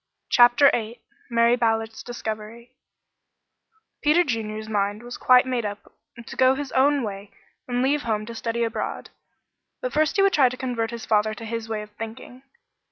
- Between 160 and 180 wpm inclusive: Yes, average, 170 wpm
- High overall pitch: Yes, high, 235 Hz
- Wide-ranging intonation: No, average, 2.7 semitones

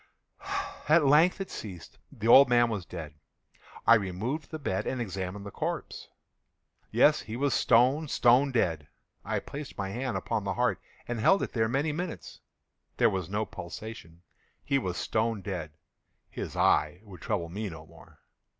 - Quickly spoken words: No, average, 165 wpm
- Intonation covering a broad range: Yes, wide, 6.2 semitones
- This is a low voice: Yes, low, 110 Hz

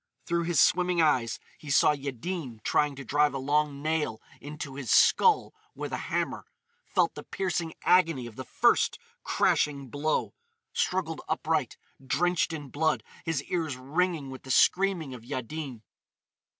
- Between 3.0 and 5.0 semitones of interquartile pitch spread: Yes, average, 4.2 semitones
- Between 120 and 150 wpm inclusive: Yes, average, 140 wpm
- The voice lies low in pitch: No, medium, 150 Hz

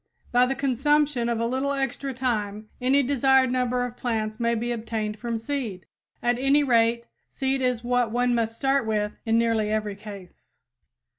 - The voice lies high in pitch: Yes, high, 240 Hz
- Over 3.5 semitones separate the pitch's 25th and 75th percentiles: No, average, 3.0 semitones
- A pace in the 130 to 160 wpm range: No, average, 170 wpm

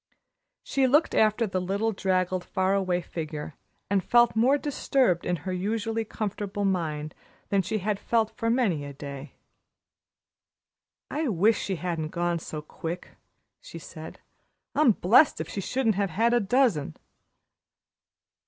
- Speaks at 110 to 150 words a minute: Yes, average, 145 wpm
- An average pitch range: Yes, average, 4.6 semitones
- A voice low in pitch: No, high, 195 Hz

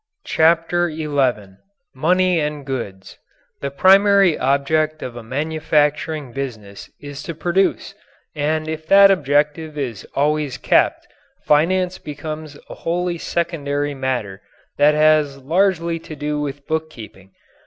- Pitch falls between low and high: Yes, medium, 150 Hz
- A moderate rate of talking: No, slow, 120 wpm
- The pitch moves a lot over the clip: No, average, 3.0 semitones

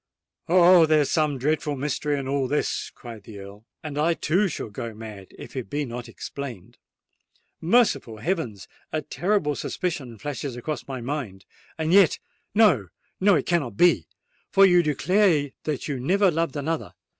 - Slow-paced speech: No, average, 155 wpm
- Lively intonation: Yes, wide, 5.7 semitones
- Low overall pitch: No, medium, 145 Hz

